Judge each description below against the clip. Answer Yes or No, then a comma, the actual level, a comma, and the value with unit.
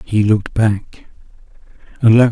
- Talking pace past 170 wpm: No, slow, 130 wpm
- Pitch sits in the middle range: No, low, 110 Hz